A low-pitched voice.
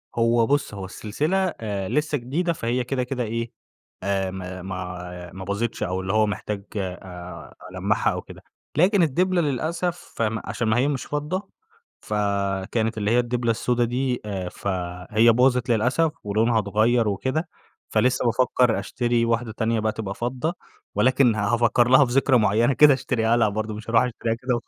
Yes: low, 115 Hz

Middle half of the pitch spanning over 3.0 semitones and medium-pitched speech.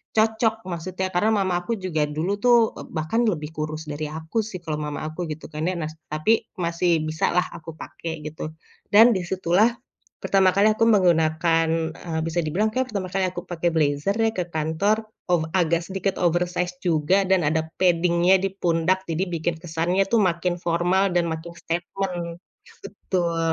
No: average, 2.7 semitones; medium, 175 Hz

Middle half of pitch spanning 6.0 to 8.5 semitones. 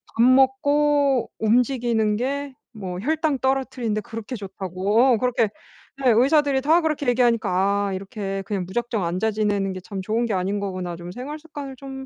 No: average, 5.1 semitones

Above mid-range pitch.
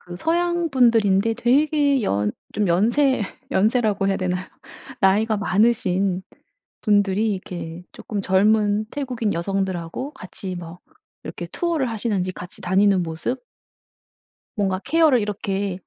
Yes: high, 205 Hz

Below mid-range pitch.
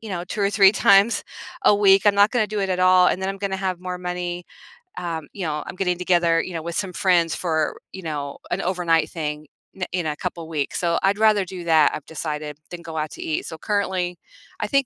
No: medium, 180 Hz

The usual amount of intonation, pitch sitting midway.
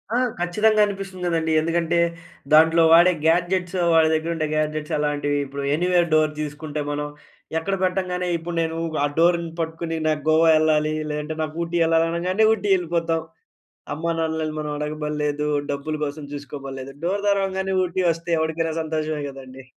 No: narrow, 2.3 semitones; medium, 160 Hz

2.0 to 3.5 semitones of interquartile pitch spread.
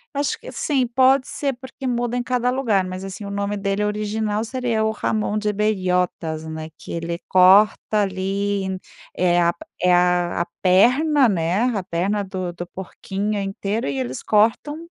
No: average, 4.2 semitones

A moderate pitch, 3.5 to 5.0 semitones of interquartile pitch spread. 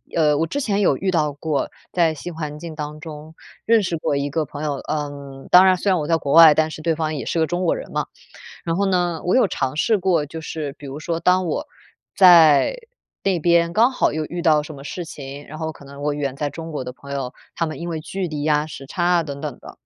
No: medium, 155 Hz; average, 3.0 semitones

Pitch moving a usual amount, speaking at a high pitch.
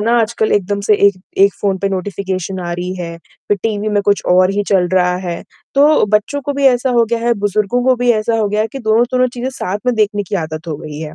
Yes: average, 3.9 semitones; high, 205 Hz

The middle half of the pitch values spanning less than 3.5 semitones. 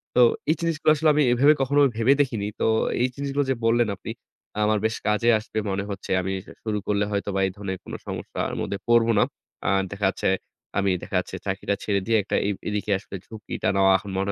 No: average, 3.8 semitones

